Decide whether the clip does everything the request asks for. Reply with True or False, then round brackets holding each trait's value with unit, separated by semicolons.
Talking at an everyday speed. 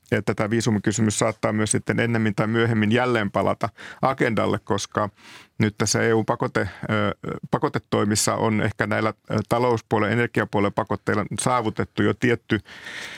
True (115 wpm)